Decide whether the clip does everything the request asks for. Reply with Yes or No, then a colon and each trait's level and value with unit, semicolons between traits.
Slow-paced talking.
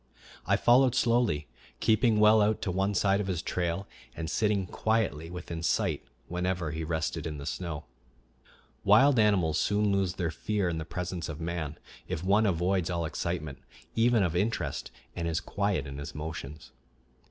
No: average, 165 wpm